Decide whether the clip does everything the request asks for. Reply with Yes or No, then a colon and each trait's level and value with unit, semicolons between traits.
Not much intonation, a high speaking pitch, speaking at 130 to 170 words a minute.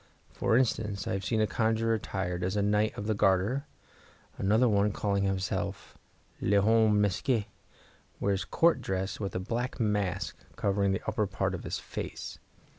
No: narrow, 2.3 semitones; low, 105 Hz; average, 160 wpm